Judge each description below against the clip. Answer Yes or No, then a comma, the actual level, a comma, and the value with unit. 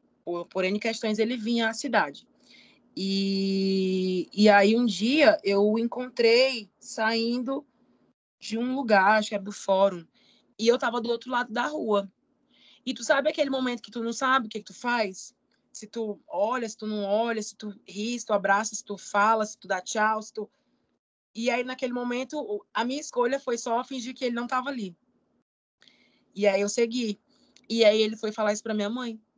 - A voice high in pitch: Yes, high, 225 Hz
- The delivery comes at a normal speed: No, fast, 195 wpm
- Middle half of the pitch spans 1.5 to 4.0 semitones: Yes, average, 3.3 semitones